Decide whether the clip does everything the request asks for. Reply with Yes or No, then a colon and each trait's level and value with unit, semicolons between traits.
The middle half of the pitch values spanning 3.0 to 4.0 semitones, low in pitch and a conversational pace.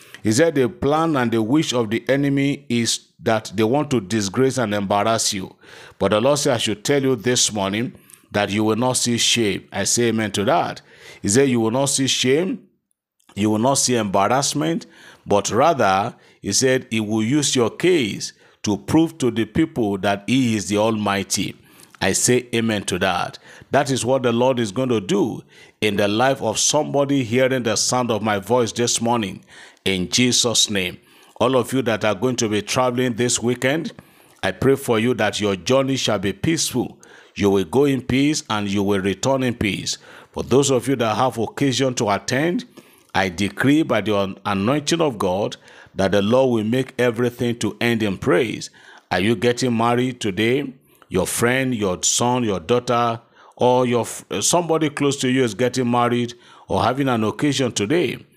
Yes: average, 3.6 semitones; low, 120 Hz; average, 190 wpm